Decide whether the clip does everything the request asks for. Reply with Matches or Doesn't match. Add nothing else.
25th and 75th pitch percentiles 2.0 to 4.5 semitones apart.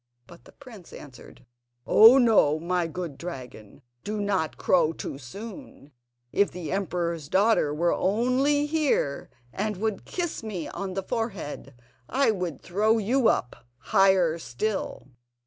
Doesn't match